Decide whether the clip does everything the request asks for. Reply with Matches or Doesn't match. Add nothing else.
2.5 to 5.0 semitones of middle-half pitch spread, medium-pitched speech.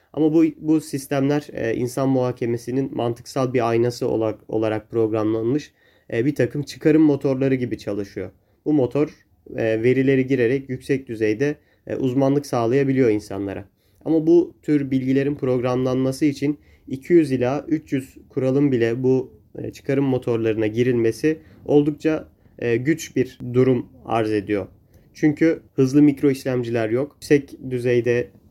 Doesn't match